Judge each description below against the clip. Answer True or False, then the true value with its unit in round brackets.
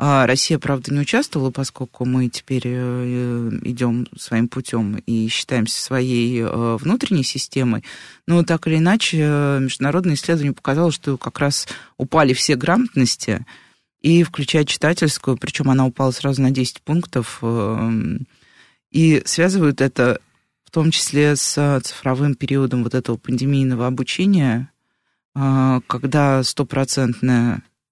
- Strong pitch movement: False (3.0 semitones)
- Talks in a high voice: False (135 Hz)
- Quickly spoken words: False (115 wpm)